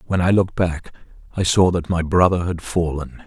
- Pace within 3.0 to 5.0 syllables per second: No, 5.2 syllables/s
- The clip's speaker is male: Yes, male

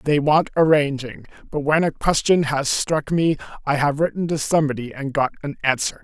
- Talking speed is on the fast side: No, average, 190 wpm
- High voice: No, medium, 150 Hz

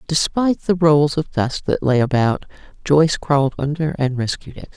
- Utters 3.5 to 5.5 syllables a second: Yes, 5.1 syllables/s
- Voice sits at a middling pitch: Yes, medium, 150 Hz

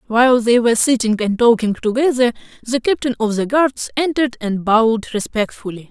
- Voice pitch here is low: No, high, 235 Hz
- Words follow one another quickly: No, average, 165 wpm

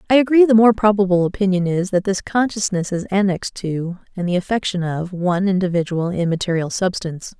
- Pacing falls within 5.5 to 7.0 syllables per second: Yes, 5.8 syllables/s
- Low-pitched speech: No, high, 190 Hz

